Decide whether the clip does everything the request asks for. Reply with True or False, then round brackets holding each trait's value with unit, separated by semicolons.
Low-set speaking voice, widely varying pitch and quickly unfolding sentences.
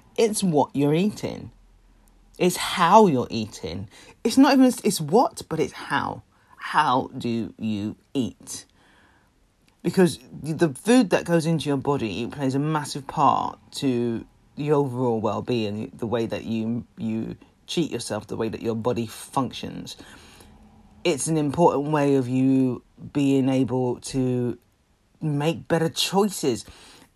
False (130 Hz; 6.5 semitones; 135 wpm)